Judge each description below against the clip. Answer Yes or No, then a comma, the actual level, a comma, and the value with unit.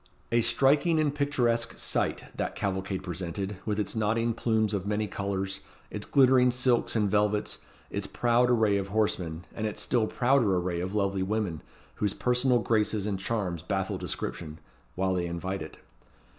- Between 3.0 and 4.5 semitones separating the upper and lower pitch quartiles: Yes, average, 3.7 semitones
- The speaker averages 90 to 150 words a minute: No, average, 160 wpm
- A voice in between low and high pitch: No, low, 105 Hz